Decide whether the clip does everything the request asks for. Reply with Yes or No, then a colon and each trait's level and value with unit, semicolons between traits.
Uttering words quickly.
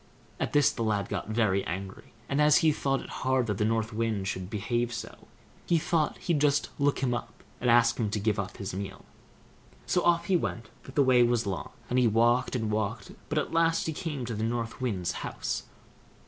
Yes: fast, 220 wpm